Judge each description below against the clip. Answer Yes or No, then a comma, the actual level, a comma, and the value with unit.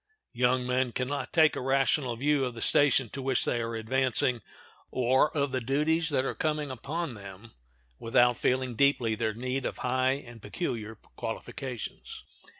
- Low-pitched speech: Yes, low, 130 Hz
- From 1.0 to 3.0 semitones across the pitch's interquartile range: Yes, narrow, 2.6 semitones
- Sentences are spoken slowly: No, average, 165 wpm